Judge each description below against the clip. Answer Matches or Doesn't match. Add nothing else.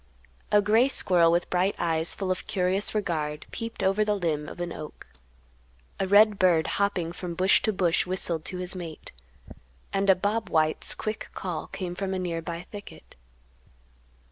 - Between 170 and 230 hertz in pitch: Matches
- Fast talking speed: Doesn't match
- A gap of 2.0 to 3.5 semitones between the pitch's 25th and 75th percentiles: Matches